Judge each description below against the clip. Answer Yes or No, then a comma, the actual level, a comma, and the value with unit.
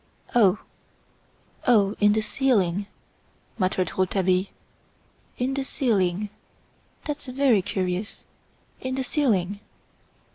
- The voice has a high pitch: Yes, high, 205 Hz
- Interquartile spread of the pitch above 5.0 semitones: Yes, wide, 5.4 semitones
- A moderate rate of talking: No, slow, 95 wpm